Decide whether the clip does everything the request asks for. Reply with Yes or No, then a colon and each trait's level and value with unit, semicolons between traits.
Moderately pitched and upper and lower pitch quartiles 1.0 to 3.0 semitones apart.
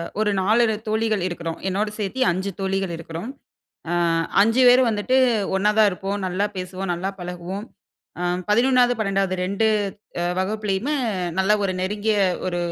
No: high, 200 Hz; average, 2.7 semitones